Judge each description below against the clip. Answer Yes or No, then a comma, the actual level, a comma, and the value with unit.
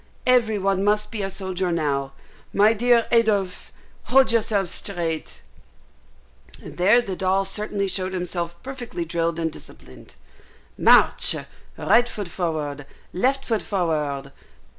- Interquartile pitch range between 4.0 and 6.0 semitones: Yes, average, 4.3 semitones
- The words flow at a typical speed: No, slow, 125 wpm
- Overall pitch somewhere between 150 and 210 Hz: Yes, high, 190 Hz